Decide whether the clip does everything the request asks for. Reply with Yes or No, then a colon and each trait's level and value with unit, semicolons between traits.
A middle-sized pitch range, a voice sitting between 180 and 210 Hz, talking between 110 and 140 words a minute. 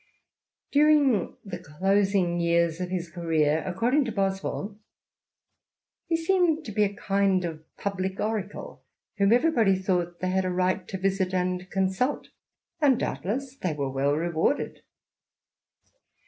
Yes: average, 3.4 semitones; high, 190 Hz; slow, 135 wpm